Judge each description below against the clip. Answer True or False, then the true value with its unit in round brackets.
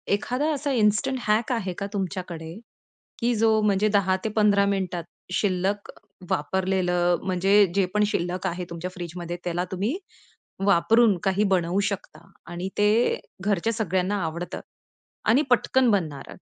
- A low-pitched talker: False (195 Hz)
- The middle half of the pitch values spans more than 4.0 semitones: False (3.0 semitones)